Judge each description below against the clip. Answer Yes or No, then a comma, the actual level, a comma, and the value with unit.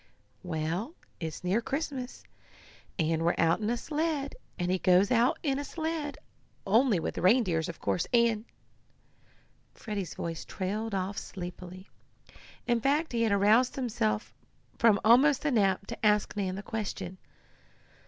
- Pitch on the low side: No, high, 210 Hz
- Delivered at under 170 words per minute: Yes, average, 145 wpm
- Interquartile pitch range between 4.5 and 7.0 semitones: Yes, wide, 5.5 semitones